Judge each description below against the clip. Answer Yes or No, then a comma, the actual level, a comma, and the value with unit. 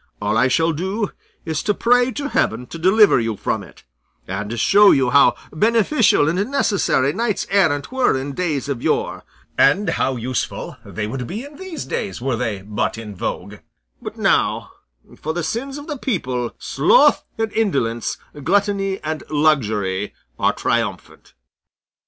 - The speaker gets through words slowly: No, average, 160 wpm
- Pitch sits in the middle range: Yes, medium, 155 Hz